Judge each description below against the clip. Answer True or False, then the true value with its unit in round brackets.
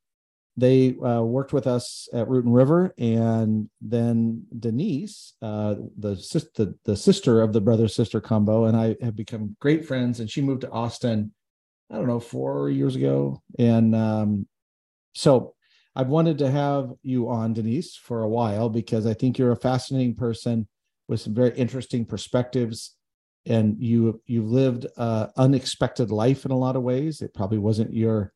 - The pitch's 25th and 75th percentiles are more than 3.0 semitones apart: False (2.6 semitones)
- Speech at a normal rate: True (175 wpm)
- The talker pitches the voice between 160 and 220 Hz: False (115 Hz)